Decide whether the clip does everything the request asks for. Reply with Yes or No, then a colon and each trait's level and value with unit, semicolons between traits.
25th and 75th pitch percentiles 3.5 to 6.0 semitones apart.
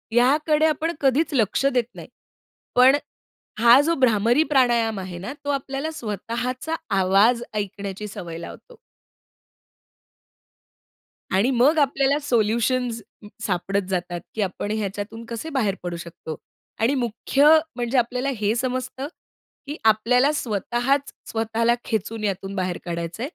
Yes: average, 4.8 semitones